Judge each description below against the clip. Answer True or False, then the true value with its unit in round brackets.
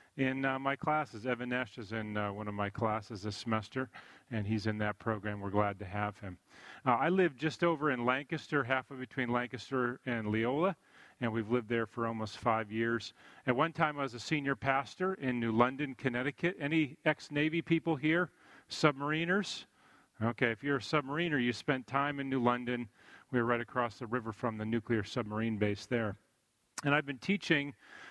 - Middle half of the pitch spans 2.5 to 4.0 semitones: False (4.6 semitones)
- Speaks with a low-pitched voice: True (125 Hz)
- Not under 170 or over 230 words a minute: True (190 wpm)